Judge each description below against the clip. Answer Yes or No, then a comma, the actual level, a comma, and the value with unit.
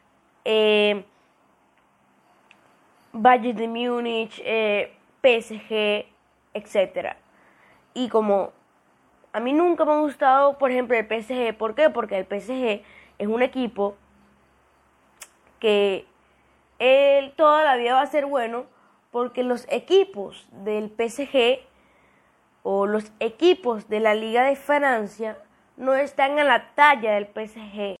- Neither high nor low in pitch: No, high, 230 Hz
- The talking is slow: Yes, slow, 120 wpm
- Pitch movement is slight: No, average, 4.4 semitones